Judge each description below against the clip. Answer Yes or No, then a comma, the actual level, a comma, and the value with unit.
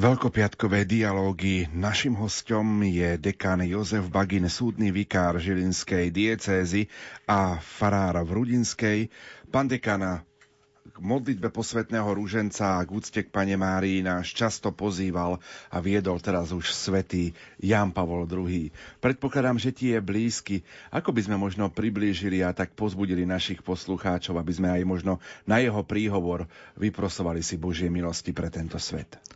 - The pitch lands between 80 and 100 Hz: Yes, very low, 95 Hz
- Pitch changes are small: No, average, 3.0 semitones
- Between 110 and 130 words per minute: No, average, 140 wpm